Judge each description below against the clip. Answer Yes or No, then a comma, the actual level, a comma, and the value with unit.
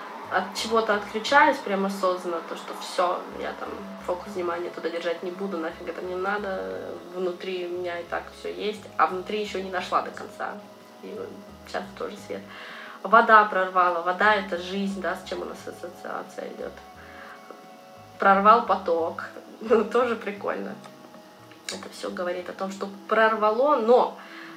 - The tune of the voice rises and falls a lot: No, average, 3.1 semitones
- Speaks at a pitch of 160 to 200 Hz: Yes, high, 190 Hz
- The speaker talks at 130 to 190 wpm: Yes, average, 155 wpm